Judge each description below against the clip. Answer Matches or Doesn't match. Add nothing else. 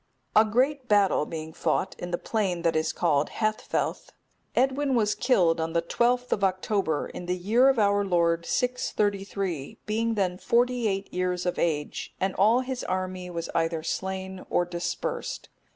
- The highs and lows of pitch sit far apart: Doesn't match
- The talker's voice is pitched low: Doesn't match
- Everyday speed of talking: Matches